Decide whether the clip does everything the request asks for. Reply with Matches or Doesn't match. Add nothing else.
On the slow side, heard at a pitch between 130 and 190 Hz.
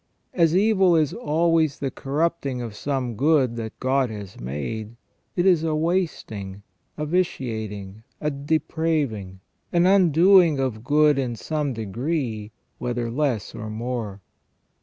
Matches